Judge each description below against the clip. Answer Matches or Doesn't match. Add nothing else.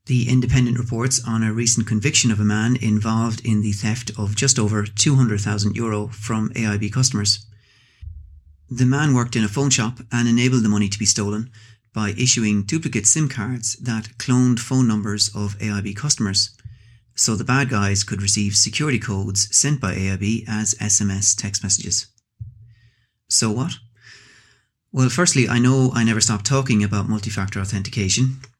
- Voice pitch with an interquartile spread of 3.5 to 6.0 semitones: Doesn't match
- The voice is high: Doesn't match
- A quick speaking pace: Doesn't match